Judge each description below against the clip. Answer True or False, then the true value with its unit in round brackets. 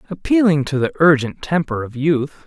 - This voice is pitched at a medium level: True (150 Hz)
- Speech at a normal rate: True (170 wpm)